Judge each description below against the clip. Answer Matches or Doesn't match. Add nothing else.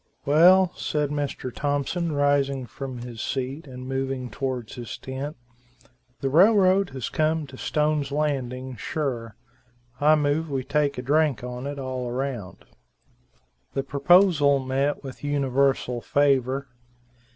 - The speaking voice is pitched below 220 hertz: Matches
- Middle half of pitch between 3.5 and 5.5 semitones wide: Doesn't match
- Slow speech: Matches